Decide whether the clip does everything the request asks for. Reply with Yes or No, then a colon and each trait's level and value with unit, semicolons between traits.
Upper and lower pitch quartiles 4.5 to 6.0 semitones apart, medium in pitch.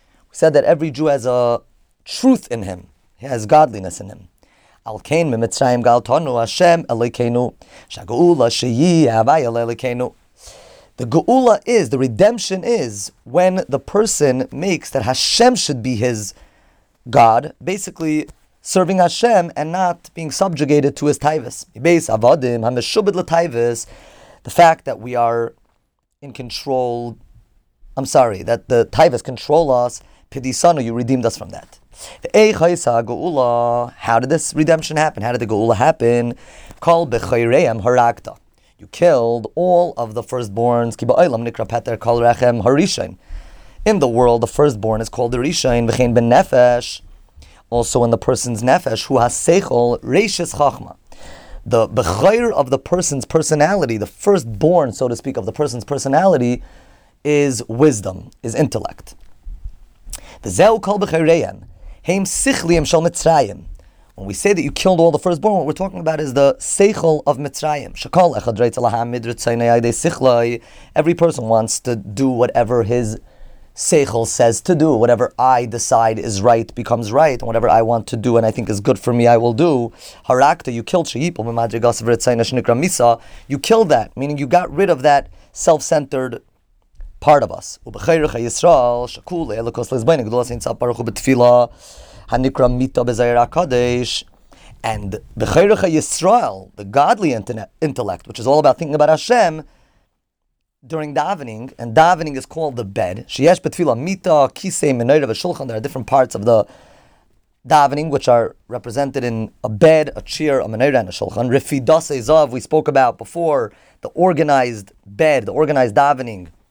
No: average, 5.1 semitones; low, 125 Hz